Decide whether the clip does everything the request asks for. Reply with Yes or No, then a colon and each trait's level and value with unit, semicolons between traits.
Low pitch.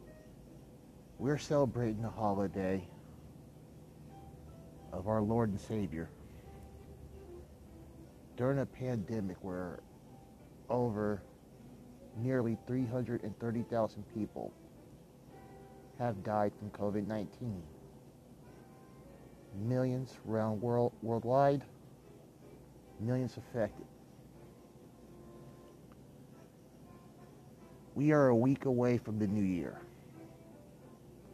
Yes: low, 110 Hz